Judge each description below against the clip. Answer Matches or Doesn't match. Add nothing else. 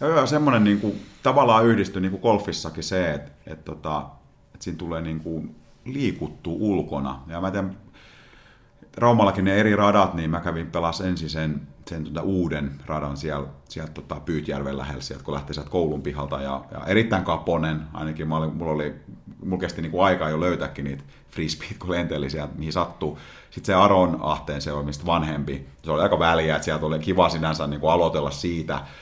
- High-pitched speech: Doesn't match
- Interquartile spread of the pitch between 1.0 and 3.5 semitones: Doesn't match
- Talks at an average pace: Doesn't match